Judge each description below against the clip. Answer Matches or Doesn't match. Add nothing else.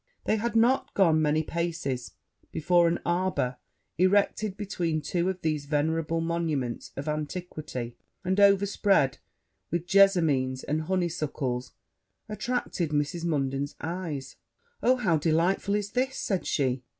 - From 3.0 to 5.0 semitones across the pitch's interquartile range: Matches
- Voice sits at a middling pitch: Matches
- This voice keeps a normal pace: Doesn't match